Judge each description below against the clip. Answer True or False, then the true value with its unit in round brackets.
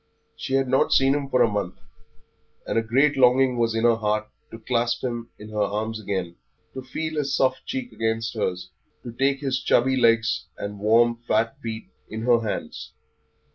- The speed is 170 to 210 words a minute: True (185 wpm)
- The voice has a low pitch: True (115 Hz)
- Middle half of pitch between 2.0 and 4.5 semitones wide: True (3.2 semitones)